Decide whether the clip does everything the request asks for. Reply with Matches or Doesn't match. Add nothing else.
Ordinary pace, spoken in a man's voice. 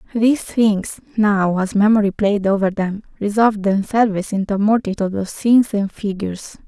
Doesn't match